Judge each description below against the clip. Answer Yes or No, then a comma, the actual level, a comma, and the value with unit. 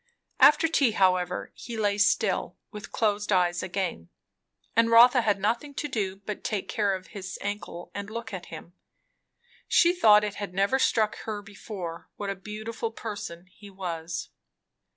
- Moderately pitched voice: No, high, 205 Hz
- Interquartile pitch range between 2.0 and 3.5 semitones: Yes, average, 3.0 semitones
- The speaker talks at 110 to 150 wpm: No, average, 160 wpm